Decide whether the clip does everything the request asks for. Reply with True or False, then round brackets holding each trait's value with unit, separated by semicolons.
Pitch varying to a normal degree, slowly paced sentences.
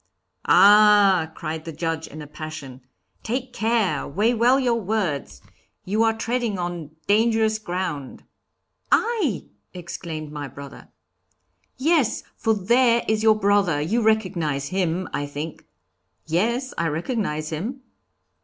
False (6.1 semitones; 125 wpm)